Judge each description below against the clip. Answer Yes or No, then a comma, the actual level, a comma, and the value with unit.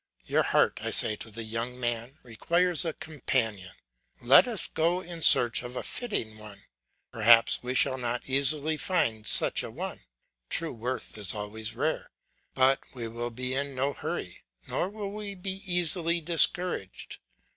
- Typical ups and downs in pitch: No, wide, 6.6 semitones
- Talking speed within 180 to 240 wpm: No, average, 160 wpm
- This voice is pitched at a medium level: No, low, 130 Hz